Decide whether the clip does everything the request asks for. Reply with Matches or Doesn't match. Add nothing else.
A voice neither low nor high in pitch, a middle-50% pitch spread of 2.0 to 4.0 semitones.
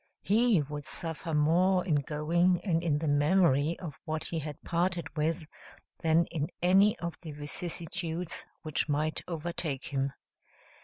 Matches